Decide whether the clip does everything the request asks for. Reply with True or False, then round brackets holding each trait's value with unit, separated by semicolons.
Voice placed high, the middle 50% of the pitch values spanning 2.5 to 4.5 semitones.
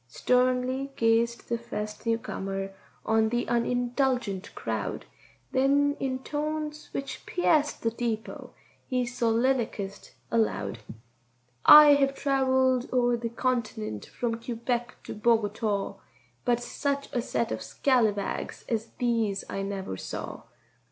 True (240 Hz; 2.9 semitones)